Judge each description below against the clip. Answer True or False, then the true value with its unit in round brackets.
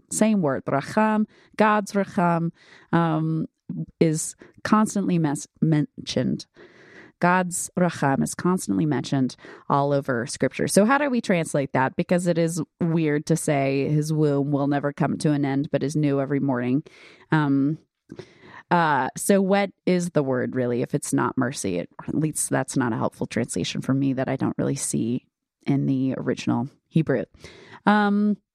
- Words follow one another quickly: False (160 wpm)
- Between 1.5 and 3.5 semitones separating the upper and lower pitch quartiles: False (4.6 semitones)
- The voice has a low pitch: False (155 Hz)